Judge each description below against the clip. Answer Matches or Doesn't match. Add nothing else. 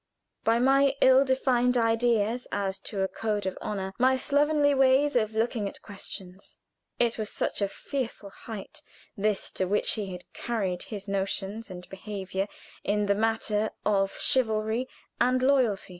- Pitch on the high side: Matches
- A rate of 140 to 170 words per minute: Matches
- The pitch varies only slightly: Doesn't match